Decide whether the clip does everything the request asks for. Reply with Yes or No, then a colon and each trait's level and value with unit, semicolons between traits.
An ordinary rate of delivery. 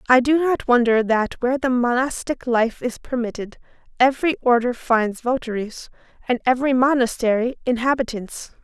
No: slow, 130 wpm